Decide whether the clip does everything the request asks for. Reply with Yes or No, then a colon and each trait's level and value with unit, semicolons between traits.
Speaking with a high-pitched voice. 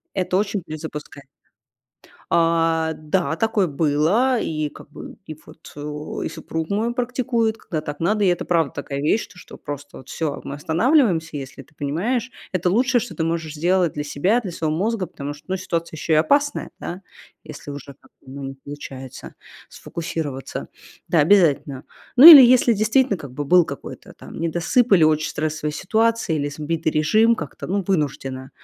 No: medium, 165 Hz